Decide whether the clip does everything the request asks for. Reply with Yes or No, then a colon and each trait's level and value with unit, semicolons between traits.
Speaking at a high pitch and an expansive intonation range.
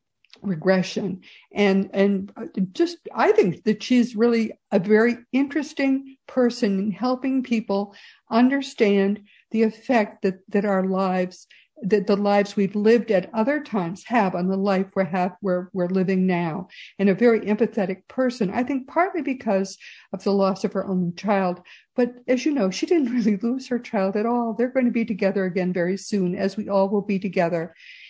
No: high, 205 Hz; average, 3.8 semitones